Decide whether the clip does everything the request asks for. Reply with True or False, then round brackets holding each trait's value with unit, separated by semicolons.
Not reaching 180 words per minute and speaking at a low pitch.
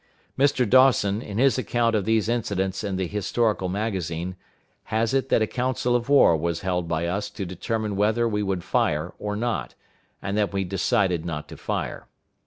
False (185 wpm; 105 Hz)